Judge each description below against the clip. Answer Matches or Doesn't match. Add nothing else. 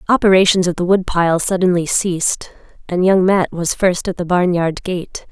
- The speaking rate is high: Doesn't match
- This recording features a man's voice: Doesn't match